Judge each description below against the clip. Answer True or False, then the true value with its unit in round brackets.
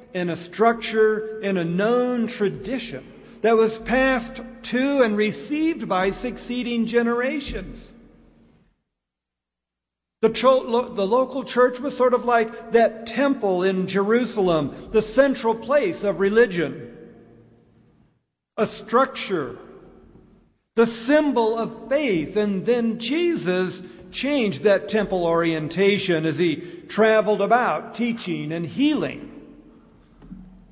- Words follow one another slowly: True (105 wpm)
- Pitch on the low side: False (225 Hz)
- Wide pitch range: False (4.5 semitones)